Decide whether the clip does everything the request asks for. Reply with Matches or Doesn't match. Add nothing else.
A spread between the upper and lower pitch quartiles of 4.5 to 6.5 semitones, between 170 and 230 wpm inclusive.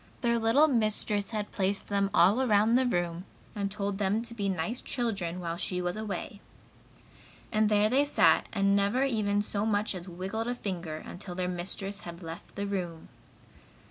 Doesn't match